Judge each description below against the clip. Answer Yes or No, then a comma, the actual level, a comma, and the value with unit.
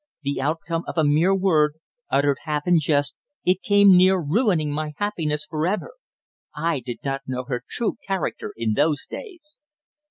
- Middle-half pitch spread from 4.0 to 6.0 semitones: Yes, average, 4.7 semitones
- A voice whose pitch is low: No, medium, 155 Hz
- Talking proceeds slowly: No, average, 165 wpm